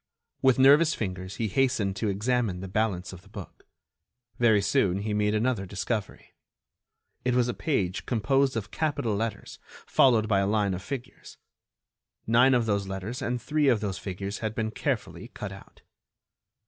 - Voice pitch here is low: Yes, low, 110 Hz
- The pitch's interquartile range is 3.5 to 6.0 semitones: Yes, average, 4.1 semitones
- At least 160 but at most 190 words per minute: Yes, average, 165 wpm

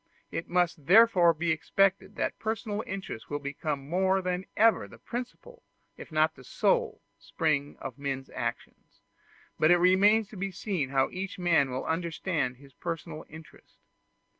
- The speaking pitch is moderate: Yes, medium, 170 Hz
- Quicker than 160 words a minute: No, average, 155 wpm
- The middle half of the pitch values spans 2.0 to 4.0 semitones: No, average, 4.8 semitones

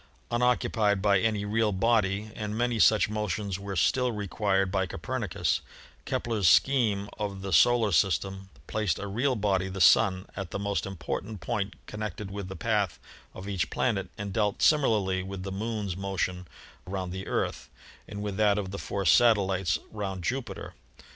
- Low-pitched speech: Yes, low, 100 Hz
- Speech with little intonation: Yes, narrow, 2.1 semitones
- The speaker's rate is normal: Yes, average, 165 wpm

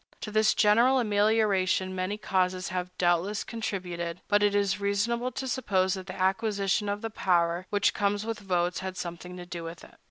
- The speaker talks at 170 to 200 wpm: Yes, average, 190 wpm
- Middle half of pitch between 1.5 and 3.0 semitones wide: Yes, narrow, 2.5 semitones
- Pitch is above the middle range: Yes, high, 195 Hz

